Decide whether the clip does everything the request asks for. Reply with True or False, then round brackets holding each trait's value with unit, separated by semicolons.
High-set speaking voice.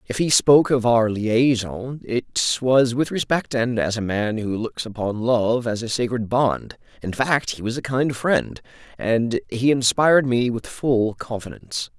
False (120 Hz)